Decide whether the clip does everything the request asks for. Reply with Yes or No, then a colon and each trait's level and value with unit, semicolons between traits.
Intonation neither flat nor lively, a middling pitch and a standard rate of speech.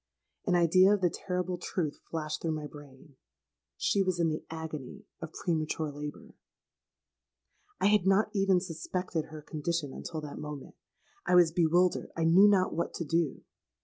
Yes: average, 3.0 semitones; medium, 165 Hz; average, 155 wpm